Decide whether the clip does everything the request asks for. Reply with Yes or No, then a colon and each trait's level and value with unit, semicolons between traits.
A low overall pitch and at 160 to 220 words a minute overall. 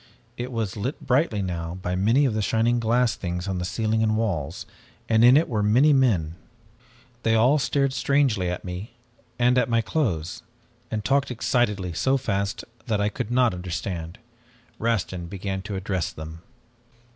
Yes: low, 110 Hz; average, 165 wpm